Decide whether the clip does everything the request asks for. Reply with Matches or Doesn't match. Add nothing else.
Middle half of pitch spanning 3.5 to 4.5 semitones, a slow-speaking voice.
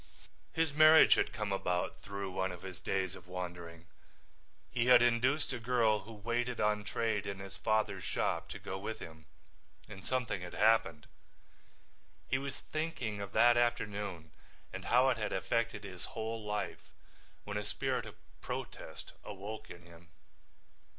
Doesn't match